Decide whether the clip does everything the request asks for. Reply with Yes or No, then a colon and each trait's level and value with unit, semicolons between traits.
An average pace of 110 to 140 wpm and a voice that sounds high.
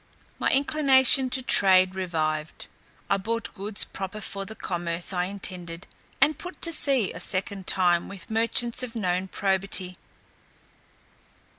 Yes: slow, 135 wpm; high, 195 Hz